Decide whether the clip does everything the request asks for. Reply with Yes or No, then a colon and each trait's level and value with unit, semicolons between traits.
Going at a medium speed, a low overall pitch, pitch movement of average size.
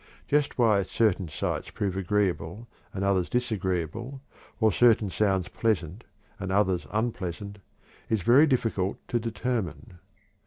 No: slow, 120 wpm; low, 105 Hz; average, 3.7 semitones